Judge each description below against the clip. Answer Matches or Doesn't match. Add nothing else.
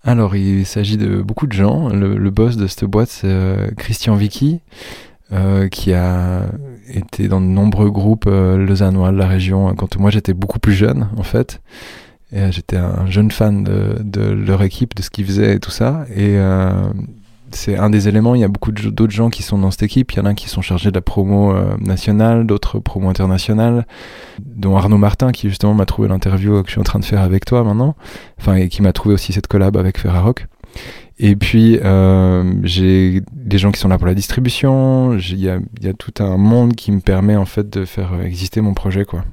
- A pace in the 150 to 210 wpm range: Doesn't match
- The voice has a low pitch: Matches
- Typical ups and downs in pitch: Doesn't match